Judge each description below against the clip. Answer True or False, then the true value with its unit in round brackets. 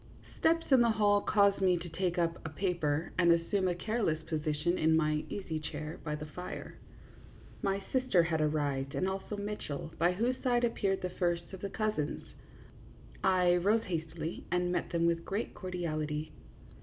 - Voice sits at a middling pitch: True (175 Hz)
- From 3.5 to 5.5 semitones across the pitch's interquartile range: True (4.0 semitones)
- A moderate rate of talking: True (170 wpm)